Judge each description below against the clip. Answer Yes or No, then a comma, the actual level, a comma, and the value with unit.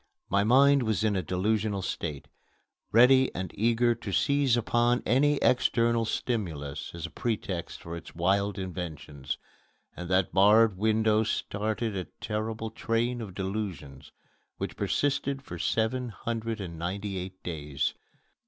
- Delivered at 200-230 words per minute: No, slow, 135 wpm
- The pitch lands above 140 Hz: No, low, 105 Hz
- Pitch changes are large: No, average, 4.1 semitones